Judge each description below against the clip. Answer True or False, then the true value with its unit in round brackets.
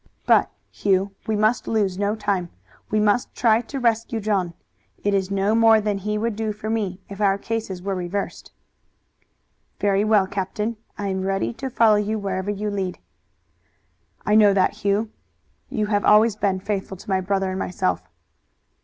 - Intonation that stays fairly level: True (1.9 semitones)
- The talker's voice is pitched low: False (205 Hz)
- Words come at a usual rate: True (170 wpm)